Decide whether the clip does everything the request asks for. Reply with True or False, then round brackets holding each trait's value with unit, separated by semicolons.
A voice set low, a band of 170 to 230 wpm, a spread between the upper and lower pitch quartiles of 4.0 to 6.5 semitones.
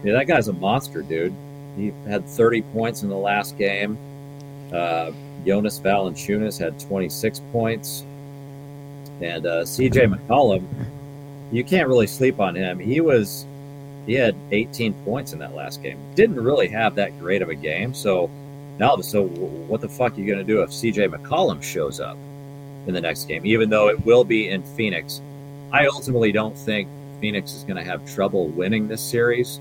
True (125 Hz; 180 wpm; 5.0 semitones)